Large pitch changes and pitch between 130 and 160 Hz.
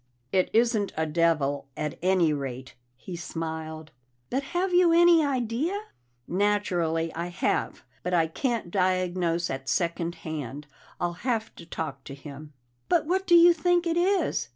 No: wide, 8.9 semitones; medium, 175 Hz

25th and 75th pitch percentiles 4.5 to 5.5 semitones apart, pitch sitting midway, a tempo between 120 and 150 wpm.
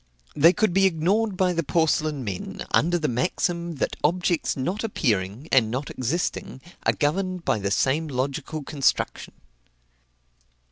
Yes: average, 5.1 semitones; medium, 155 Hz; average, 140 wpm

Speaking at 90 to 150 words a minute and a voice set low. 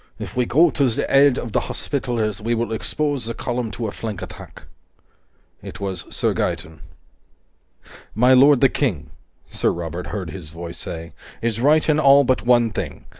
No: average, 175 wpm; low, 115 Hz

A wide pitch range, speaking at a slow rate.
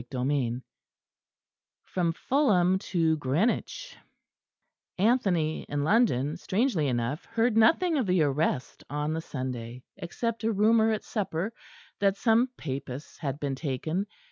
Yes: wide, 7.7 semitones; slow, 125 wpm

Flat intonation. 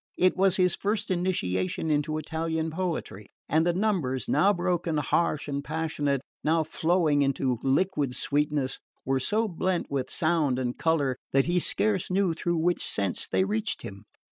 No: average, 4.5 semitones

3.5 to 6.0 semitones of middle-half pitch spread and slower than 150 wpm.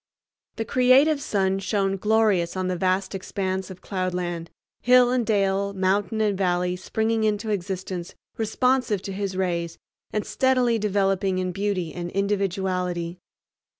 No: narrow, 2.6 semitones; slow, 135 wpm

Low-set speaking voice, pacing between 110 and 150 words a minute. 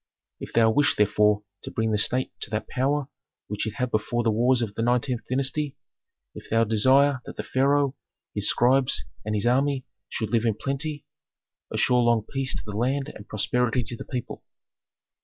No: low, 120 Hz; average, 185 wpm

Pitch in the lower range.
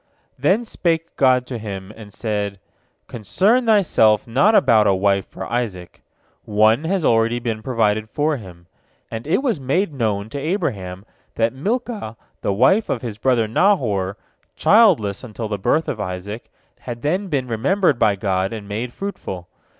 Yes: low, 115 Hz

